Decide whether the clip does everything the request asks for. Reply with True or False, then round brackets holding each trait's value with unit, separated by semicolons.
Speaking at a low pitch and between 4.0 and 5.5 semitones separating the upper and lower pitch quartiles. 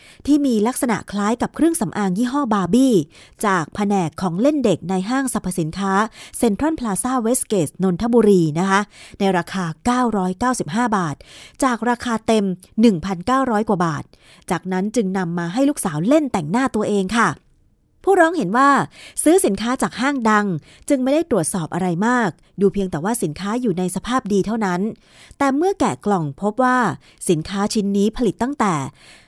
False (210 Hz; 4.8 semitones)